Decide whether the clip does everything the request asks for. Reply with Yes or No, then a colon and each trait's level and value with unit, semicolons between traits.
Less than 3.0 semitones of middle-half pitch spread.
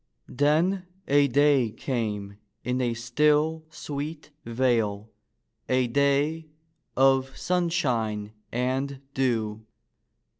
No: average, 4.2 semitones